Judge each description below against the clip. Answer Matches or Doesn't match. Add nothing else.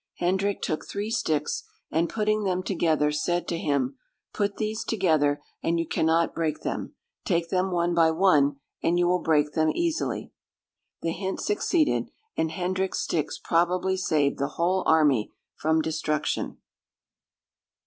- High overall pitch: Doesn't match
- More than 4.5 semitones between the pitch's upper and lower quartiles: Doesn't match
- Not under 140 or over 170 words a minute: Matches